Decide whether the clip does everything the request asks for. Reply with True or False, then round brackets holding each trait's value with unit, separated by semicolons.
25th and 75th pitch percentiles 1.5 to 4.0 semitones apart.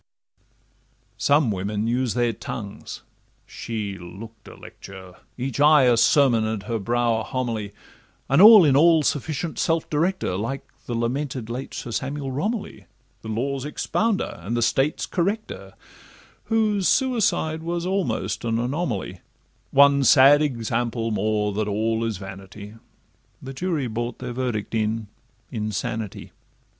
False (5.1 semitones)